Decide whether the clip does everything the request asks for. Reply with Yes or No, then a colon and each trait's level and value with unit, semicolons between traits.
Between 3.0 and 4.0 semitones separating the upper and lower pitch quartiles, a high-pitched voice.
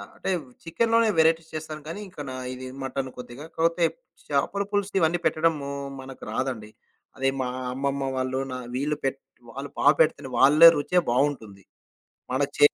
No: average, 3.7 semitones; medium, 145 Hz